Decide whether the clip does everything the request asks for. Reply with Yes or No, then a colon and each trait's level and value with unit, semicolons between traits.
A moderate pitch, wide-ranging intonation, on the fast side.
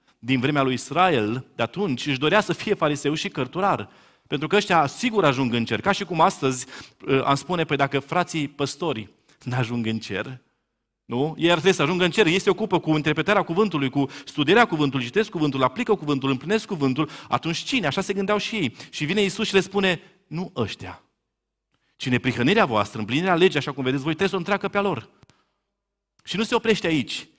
Yes: medium, 155 Hz; wide, 6.3 semitones; fast, 205 wpm